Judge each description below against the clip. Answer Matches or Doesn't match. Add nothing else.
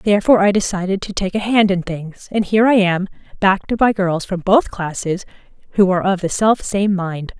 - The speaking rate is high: Matches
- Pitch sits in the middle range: Doesn't match